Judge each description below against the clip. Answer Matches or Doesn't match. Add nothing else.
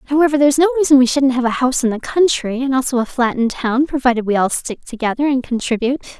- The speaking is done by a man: Doesn't match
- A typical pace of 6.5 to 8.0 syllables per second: Matches